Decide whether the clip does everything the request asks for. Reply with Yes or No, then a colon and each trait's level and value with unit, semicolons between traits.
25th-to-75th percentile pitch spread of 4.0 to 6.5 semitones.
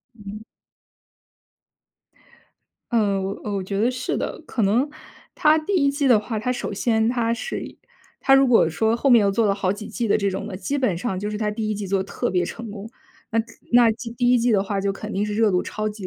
No: average, 3.2 semitones